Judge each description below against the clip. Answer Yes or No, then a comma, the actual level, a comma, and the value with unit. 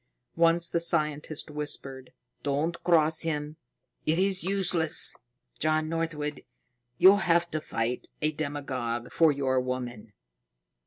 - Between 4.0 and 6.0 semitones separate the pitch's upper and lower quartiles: No, average, 3.1 semitones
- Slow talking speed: Yes, slow, 115 wpm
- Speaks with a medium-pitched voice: Yes, medium, 155 Hz